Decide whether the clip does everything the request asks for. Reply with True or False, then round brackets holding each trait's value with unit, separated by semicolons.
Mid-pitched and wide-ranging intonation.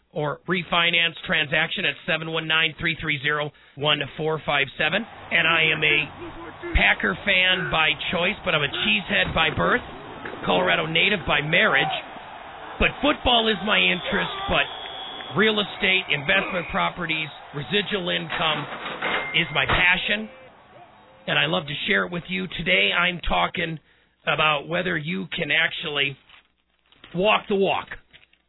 False (170 Hz; 3.7 semitones)